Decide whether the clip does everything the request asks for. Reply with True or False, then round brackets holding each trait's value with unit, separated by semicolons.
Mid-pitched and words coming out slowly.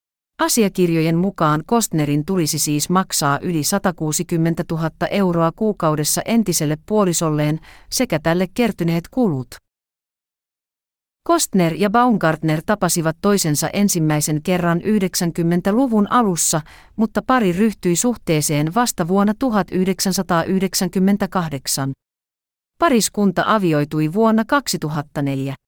True (175 Hz; 85 wpm)